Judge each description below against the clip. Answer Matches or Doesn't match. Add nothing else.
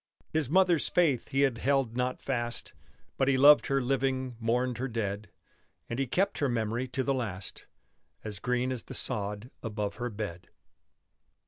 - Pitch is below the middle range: Matches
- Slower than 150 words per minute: Doesn't match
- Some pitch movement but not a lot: Matches